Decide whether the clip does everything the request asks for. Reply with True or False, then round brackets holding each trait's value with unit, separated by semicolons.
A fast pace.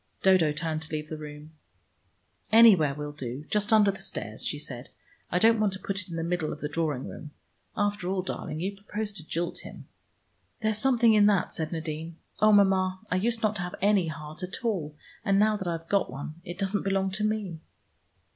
True (210 wpm)